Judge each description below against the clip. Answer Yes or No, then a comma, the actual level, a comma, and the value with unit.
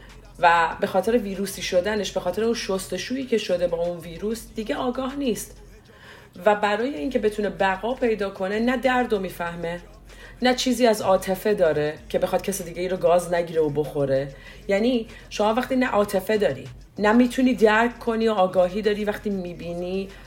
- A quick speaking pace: No, average, 170 wpm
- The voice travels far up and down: No, average, 4.2 semitones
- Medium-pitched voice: No, high, 195 Hz